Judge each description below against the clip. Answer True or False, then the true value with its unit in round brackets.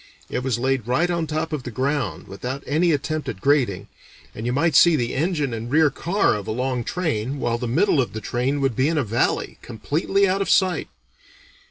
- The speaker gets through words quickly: True (215 wpm)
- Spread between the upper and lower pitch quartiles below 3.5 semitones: False (4.7 semitones)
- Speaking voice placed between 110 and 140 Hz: True (135 Hz)